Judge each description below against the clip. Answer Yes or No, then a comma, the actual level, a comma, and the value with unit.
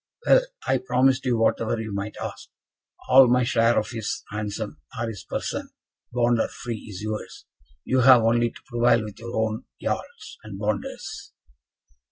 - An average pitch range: No, narrow, 2.1 semitones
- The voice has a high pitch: No, low, 115 Hz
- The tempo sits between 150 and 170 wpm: Yes, average, 165 wpm